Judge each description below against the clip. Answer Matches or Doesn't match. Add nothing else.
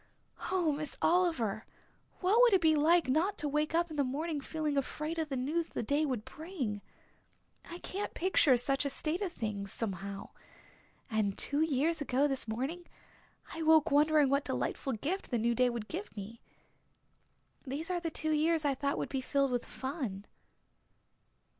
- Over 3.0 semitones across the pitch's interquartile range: Matches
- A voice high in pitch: Matches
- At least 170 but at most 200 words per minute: Matches